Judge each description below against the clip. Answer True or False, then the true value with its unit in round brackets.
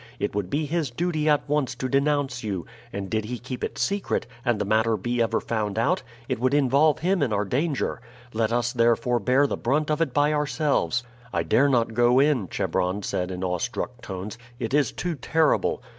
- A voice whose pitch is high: False (125 Hz)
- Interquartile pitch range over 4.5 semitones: True (5.0 semitones)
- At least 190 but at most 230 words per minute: True (205 wpm)